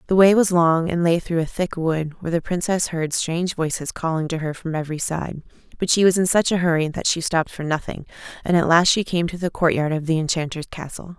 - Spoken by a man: No, female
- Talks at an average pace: No, fast, 245 wpm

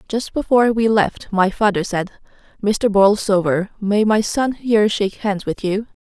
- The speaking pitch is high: Yes, high, 205 Hz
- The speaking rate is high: No, average, 170 wpm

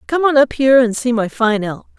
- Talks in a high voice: Yes, high, 245 Hz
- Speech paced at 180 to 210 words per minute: No, fast, 270 wpm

